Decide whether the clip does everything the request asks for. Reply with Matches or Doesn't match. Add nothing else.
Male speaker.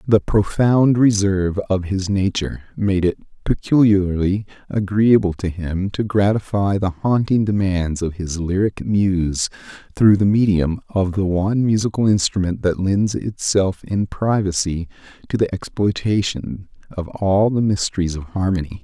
Matches